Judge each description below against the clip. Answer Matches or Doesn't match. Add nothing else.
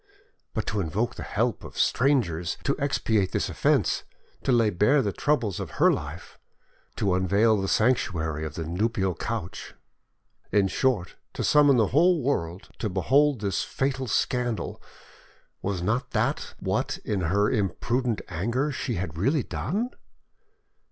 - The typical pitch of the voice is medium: Doesn't match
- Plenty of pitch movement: Matches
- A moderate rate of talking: Matches